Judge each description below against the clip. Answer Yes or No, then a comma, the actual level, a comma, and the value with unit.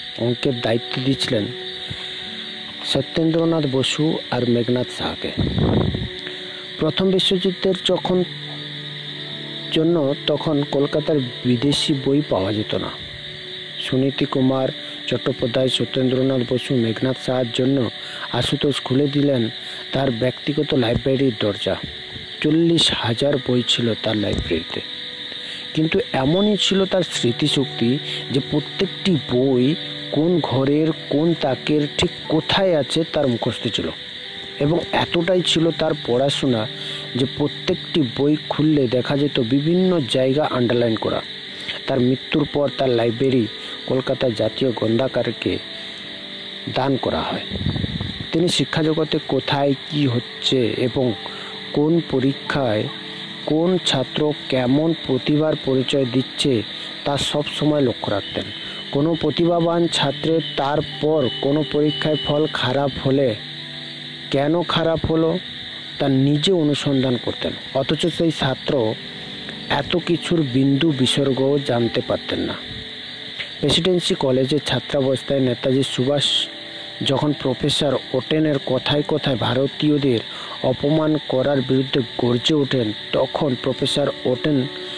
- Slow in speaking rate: Yes, slow, 105 wpm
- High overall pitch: No, medium, 140 Hz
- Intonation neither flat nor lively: Yes, average, 3.3 semitones